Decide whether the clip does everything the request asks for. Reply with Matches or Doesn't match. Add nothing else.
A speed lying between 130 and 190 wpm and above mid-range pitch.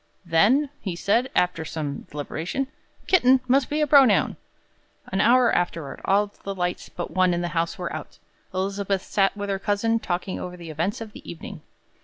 Matches